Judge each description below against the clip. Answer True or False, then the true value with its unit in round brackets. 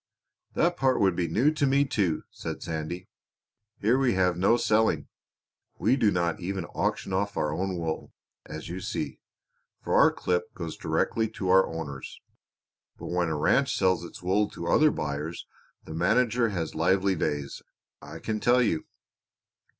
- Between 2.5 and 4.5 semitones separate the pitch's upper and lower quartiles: False (5.0 semitones)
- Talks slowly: False (165 wpm)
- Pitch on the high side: False (95 Hz)